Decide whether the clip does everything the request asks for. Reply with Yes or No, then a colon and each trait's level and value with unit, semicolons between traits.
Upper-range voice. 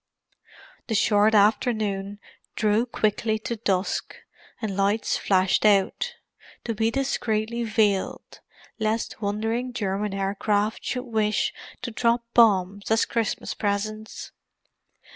Yes: high, 215 Hz